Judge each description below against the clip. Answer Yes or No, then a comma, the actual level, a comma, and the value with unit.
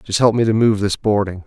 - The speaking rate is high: Yes, fast, 285 wpm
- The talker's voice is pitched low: Yes, low, 105 Hz